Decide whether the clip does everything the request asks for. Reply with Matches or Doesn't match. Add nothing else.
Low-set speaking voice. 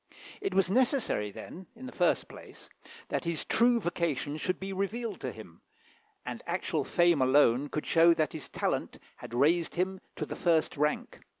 Doesn't match